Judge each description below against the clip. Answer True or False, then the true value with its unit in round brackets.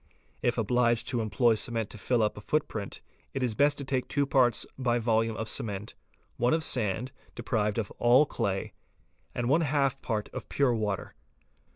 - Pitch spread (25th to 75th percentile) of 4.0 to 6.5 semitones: False (3.2 semitones)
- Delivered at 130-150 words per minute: False (180 wpm)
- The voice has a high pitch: False (120 Hz)